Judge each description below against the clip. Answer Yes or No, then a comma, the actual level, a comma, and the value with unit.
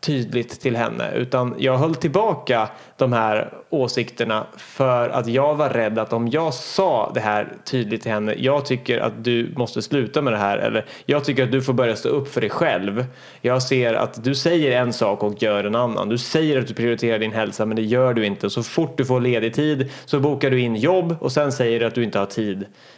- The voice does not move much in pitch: No, average, 3.6 semitones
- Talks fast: Yes, fast, 230 wpm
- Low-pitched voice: Yes, low, 125 Hz